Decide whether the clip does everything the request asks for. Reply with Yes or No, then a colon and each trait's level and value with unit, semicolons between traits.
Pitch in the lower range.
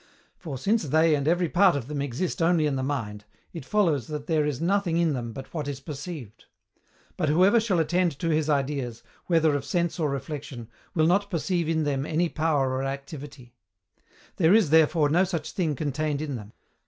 No: medium, 155 Hz